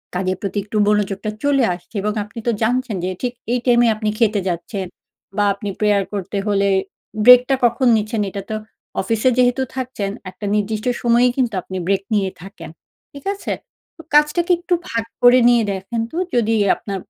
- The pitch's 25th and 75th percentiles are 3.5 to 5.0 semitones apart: Yes, average, 3.8 semitones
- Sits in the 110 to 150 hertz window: No, high, 215 Hz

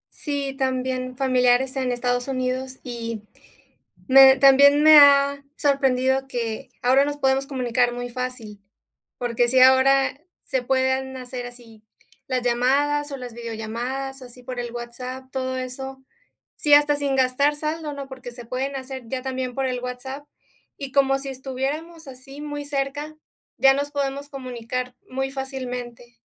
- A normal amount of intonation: No, narrow, 1.6 semitones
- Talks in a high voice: Yes, very high, 260 Hz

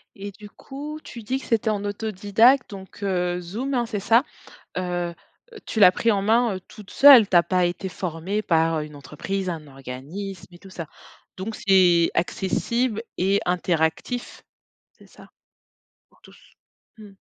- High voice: Yes, high, 195 Hz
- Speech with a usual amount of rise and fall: Yes, average, 3.9 semitones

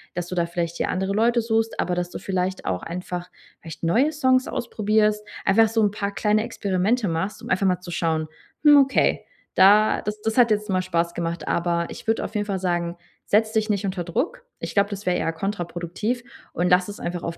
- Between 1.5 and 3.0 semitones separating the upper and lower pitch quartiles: No, average, 3.7 semitones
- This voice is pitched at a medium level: No, high, 195 Hz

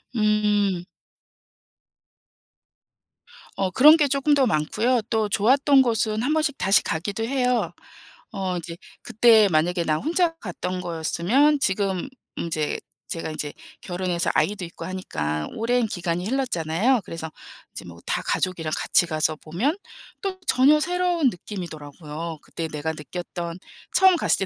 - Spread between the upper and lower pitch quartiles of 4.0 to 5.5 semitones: No, wide, 7.2 semitones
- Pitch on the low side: No, high, 195 Hz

